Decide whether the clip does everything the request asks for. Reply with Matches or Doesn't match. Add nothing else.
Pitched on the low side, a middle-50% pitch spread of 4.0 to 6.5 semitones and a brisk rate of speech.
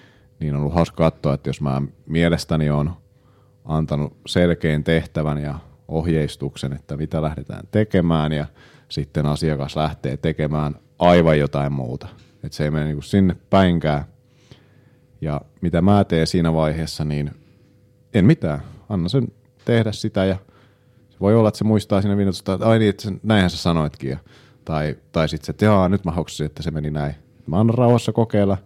Matches